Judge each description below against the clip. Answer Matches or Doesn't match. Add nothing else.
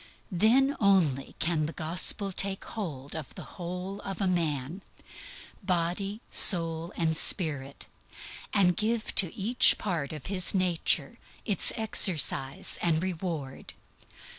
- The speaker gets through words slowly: Matches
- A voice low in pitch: Doesn't match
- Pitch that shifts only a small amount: Doesn't match